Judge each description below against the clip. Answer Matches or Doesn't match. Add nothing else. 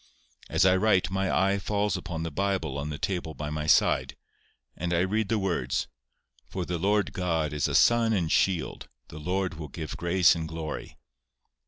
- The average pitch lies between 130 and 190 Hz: Doesn't match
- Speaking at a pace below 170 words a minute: Doesn't match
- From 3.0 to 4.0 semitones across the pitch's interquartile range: Matches